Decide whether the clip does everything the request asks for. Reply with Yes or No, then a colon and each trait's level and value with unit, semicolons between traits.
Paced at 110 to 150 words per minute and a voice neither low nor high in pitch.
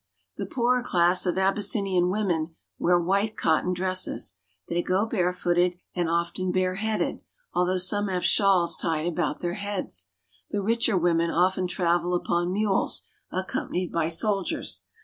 Yes: average, 140 wpm; medium, 180 Hz